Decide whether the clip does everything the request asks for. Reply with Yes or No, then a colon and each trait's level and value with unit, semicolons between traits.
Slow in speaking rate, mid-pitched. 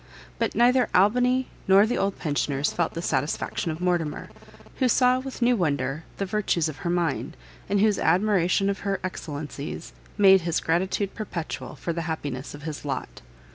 No: average, 170 wpm; medium, 180 Hz